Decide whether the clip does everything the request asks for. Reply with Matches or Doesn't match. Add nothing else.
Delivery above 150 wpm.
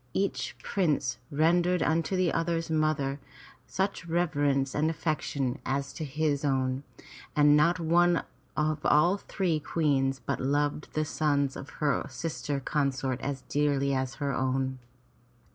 Doesn't match